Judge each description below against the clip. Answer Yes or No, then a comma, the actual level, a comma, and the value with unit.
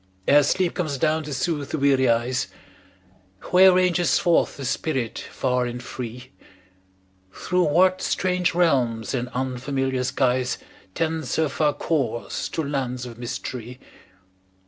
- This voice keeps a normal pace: No, slow, 130 wpm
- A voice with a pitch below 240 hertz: Yes, low, 135 Hz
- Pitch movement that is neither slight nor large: Yes, average, 4.4 semitones